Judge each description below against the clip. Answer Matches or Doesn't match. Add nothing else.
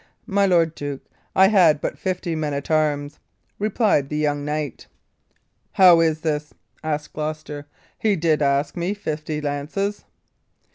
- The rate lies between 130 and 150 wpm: Matches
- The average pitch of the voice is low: Doesn't match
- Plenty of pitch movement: Doesn't match